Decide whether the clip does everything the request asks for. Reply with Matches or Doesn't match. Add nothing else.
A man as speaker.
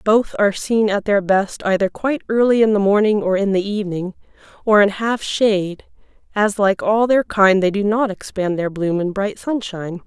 Doesn't match